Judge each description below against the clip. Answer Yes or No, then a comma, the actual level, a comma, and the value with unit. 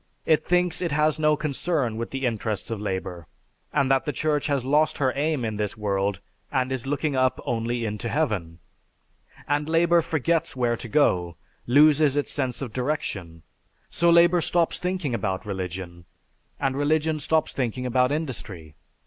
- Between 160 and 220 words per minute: Yes, average, 165 wpm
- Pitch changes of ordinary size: No, wide, 6.0 semitones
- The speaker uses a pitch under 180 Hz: Yes, low, 135 Hz